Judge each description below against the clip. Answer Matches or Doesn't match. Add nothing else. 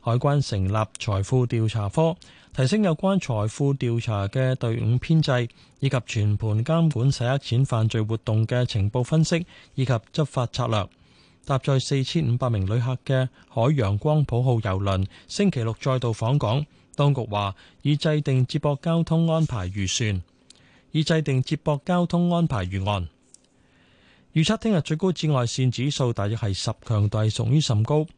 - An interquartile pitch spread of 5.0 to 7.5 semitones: Matches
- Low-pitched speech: Matches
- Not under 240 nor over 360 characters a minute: Matches